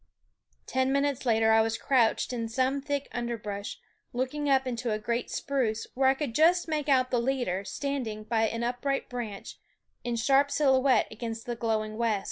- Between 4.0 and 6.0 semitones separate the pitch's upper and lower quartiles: No, average, 3.3 semitones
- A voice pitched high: Yes, high, 245 Hz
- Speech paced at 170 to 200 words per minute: Yes, average, 175 wpm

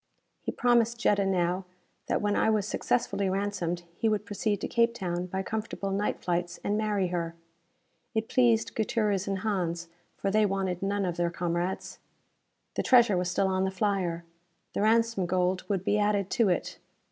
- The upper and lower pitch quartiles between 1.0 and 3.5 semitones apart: Yes, average, 3.0 semitones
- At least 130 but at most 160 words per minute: No, average, 175 wpm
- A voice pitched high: Yes, high, 195 Hz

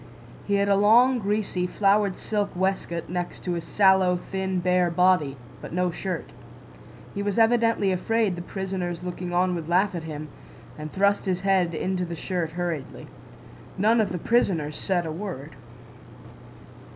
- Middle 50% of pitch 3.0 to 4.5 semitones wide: No, narrow, 2.5 semitones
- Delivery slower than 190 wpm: Yes, average, 160 wpm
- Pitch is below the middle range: No, medium, 185 Hz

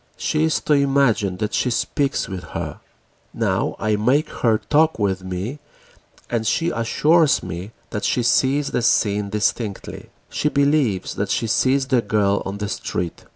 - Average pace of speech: Yes, average, 155 wpm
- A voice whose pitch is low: Yes, low, 115 Hz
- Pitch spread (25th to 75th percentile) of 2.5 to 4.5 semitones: No, wide, 5.5 semitones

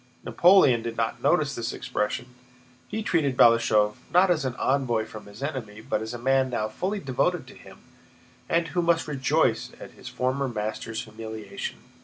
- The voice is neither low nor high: No, low, 125 Hz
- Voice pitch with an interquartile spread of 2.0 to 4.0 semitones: No, average, 4.8 semitones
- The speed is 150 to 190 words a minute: Yes, average, 170 wpm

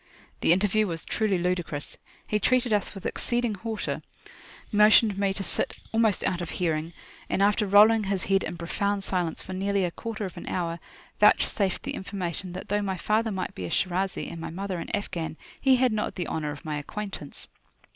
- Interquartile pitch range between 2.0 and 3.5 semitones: Yes, average, 3.2 semitones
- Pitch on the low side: No, high, 195 Hz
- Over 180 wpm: Yes, average, 195 wpm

